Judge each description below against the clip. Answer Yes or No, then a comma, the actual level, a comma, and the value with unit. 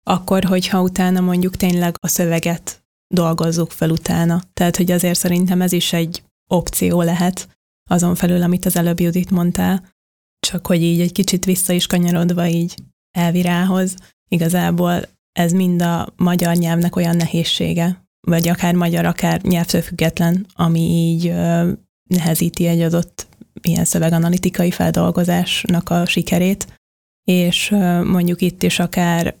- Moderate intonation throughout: No, narrow, 1.1 semitones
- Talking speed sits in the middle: Yes, average, 130 wpm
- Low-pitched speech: No, medium, 175 Hz